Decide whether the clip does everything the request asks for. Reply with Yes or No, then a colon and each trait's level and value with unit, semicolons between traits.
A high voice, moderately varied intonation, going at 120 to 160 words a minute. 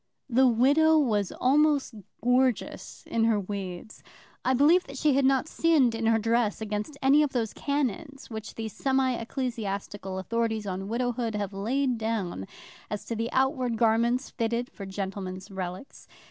Yes: high, 230 Hz; average, 4.2 semitones; average, 155 wpm